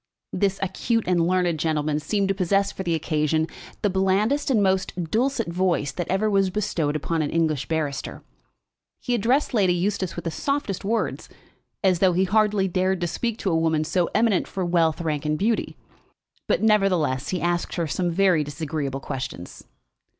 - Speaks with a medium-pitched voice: Yes, medium, 180 Hz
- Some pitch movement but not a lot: Yes, average, 3.9 semitones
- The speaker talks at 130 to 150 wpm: No, average, 175 wpm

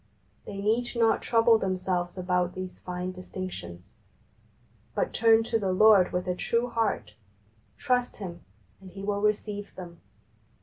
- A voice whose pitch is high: Yes, high, 195 Hz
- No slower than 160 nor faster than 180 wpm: No, average, 145 wpm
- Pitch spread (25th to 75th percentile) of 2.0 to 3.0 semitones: No, average, 3.6 semitones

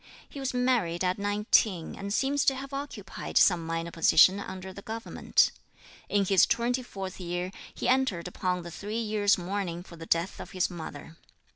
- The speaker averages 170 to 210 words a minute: Yes, average, 175 wpm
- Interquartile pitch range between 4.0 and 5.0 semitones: Yes, average, 4.5 semitones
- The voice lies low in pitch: No, high, 195 Hz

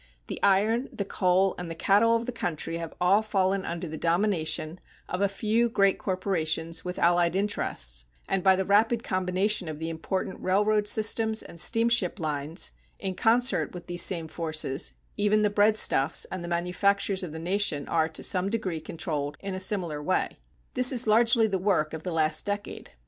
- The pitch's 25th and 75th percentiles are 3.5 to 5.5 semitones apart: Yes, average, 3.9 semitones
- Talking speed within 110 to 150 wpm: No, average, 180 wpm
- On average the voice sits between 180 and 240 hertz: Yes, medium, 185 Hz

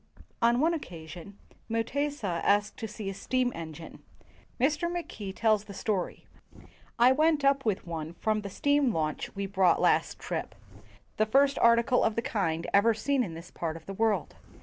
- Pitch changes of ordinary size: No, wide, 5.7 semitones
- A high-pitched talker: Yes, high, 215 Hz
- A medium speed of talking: Yes, average, 185 wpm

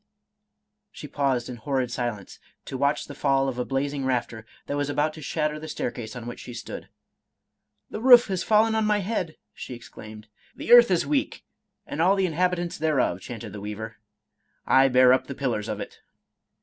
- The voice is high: No, medium, 140 Hz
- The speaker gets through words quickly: Yes, fast, 210 wpm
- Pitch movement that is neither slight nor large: No, wide, 5.9 semitones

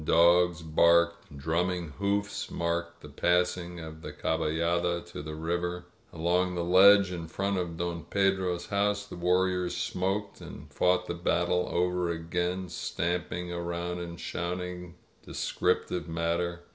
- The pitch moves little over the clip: Yes, narrow, 1.1 semitones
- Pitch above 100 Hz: No, very low, 85 Hz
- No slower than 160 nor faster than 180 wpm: No, slow, 135 wpm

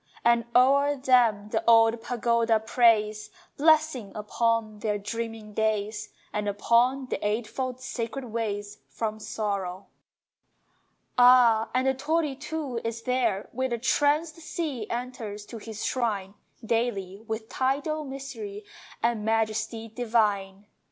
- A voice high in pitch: Yes, high, 230 Hz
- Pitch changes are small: No, average, 3.3 semitones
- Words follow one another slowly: Yes, slow, 120 wpm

